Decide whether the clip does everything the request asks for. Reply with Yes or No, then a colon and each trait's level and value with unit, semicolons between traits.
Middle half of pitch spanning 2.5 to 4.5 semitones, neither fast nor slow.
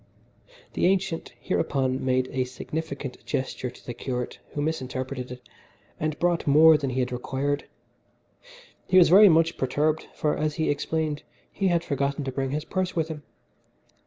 Yes: average, 3.6 semitones; average, 160 wpm